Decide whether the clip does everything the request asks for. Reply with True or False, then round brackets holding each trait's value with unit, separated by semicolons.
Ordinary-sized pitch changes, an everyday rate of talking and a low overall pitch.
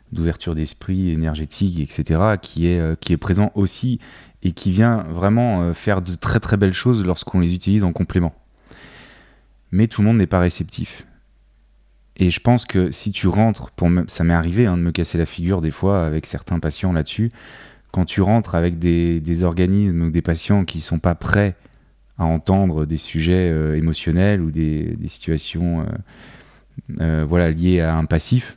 True (3.5 semitones; 185 wpm; 90 Hz)